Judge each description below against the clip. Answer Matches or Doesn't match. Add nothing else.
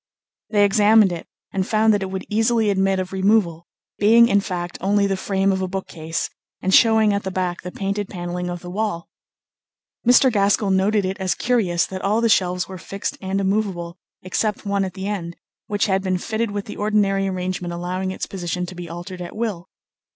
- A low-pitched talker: Doesn't match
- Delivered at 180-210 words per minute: Matches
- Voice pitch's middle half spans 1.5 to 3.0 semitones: Matches